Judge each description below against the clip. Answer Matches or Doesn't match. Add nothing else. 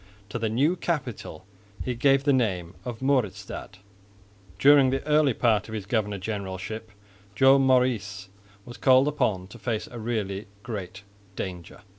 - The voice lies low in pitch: Matches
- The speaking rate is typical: Matches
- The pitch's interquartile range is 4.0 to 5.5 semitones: Matches